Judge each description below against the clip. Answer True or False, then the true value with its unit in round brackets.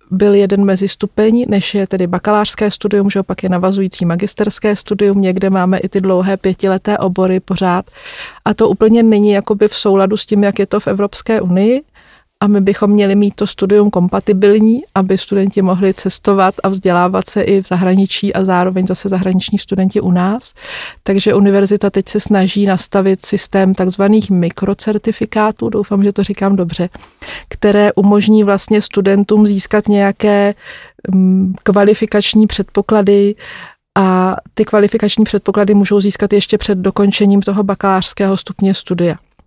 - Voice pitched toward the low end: False (200 Hz)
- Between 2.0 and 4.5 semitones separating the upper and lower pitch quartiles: False (1.4 semitones)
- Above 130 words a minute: True (150 wpm)